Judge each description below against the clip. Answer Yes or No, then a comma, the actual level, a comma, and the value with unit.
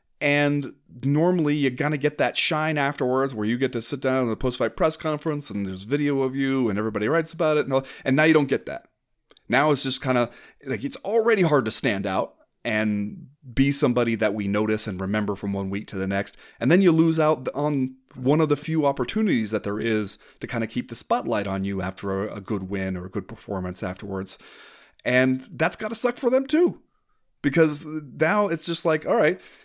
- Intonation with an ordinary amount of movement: No, wide, 6.3 semitones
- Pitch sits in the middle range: No, low, 130 Hz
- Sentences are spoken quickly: Yes, fast, 225 wpm